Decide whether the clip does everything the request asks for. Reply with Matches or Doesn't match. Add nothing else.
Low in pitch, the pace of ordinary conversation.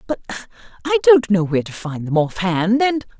Doesn't match